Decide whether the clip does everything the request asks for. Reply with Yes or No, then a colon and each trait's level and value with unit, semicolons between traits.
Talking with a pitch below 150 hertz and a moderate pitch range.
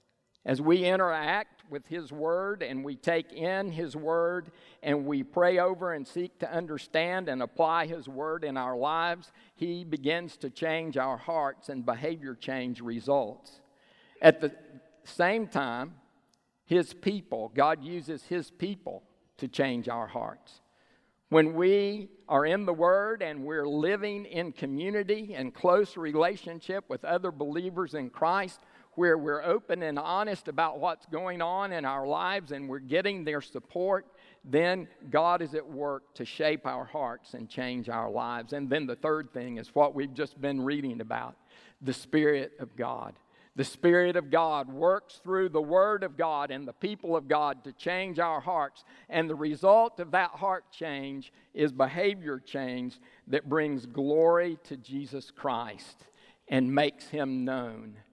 No: medium, 160 Hz; average, 4.2 semitones